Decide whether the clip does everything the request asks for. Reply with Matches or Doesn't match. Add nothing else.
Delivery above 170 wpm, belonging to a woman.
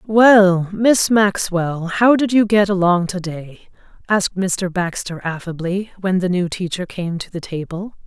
Doesn't match